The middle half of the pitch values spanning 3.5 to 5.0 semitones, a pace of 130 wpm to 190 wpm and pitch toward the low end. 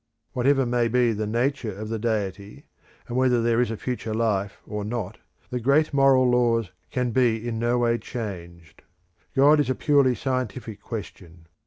No: average, 3.0 semitones; average, 170 wpm; low, 120 Hz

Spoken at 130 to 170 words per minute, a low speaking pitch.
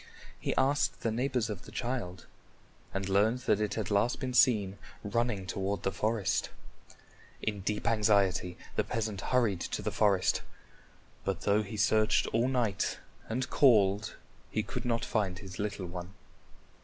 Yes: average, 155 wpm; low, 105 Hz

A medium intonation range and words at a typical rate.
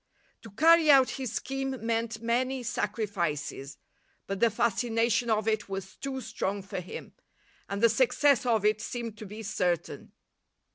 Yes: average, 3.6 semitones; average, 150 wpm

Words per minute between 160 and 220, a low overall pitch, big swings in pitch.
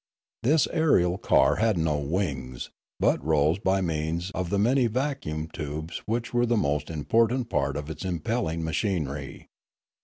No: average, 150 wpm; very low, 85 Hz; wide, 6.9 semitones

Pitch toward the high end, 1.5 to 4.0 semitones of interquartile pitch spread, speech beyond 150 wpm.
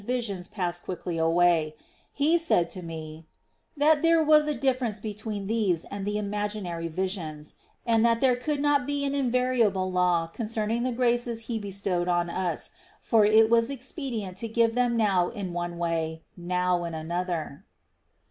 No: high, 205 Hz; wide, 5.5 semitones; average, 160 wpm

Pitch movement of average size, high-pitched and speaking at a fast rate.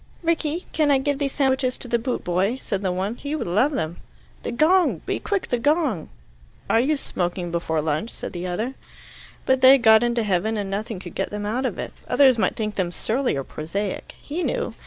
No: wide, 6.5 semitones; high, 230 Hz; fast, 220 wpm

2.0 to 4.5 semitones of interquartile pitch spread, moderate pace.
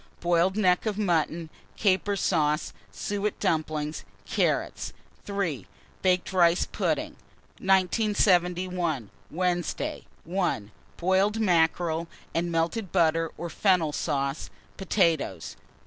No: average, 2.8 semitones; slow, 95 wpm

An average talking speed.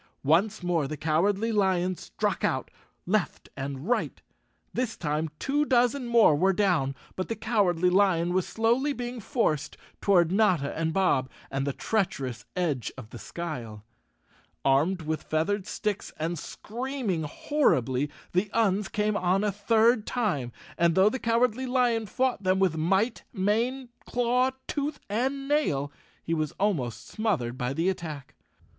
Yes: average, 150 wpm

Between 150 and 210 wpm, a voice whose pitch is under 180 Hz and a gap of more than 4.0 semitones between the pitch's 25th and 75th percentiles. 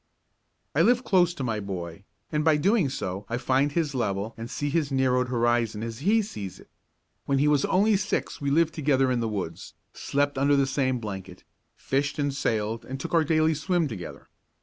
Yes: average, 195 wpm; low, 135 Hz; average, 5.2 semitones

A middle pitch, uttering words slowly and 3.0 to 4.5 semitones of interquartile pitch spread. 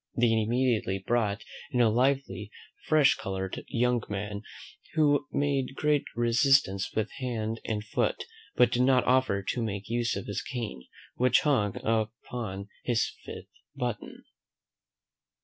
No: low, 115 Hz; slow, 130 wpm; average, 3.6 semitones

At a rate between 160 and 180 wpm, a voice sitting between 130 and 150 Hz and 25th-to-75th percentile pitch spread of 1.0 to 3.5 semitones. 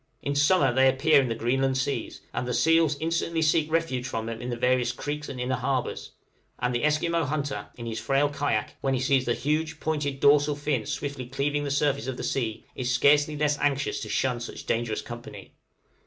No: fast, 205 wpm; medium, 140 Hz; average, 3.0 semitones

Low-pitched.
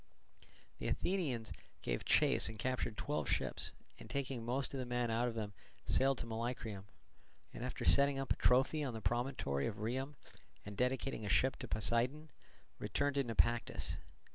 Yes: low, 125 Hz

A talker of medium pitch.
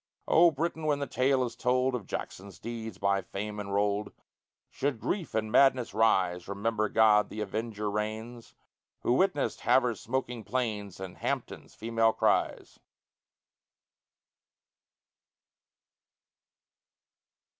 No: low, 110 Hz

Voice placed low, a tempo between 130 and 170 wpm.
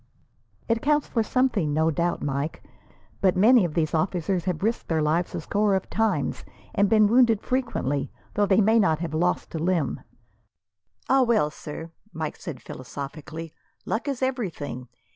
No: medium, 180 Hz; average, 160 wpm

